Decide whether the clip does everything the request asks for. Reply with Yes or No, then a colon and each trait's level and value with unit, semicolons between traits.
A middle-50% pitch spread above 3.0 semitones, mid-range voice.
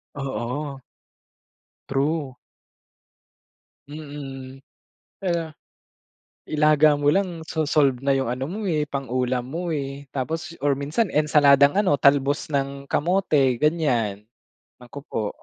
No: narrow, 2.5 semitones; medium, 145 Hz